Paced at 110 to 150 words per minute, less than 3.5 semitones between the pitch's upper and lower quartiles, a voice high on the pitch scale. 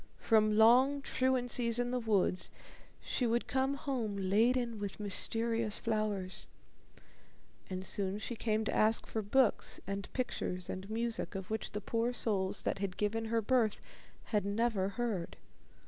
Yes: average, 145 wpm; average, 3.0 semitones; high, 220 Hz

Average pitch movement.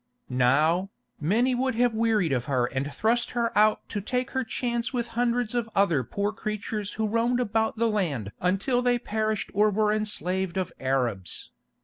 Yes: average, 4.5 semitones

